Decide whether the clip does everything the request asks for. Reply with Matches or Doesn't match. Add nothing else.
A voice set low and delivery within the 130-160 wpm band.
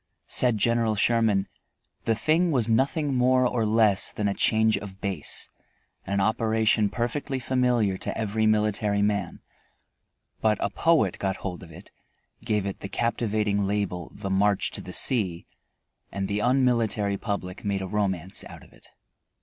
Matches